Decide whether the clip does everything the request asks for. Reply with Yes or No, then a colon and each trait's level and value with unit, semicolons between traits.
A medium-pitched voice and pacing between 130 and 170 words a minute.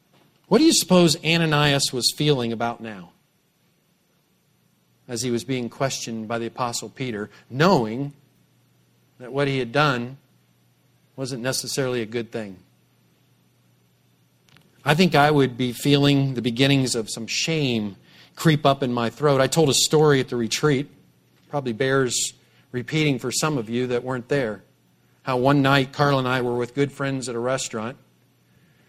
No: low, 130 Hz; average, 155 wpm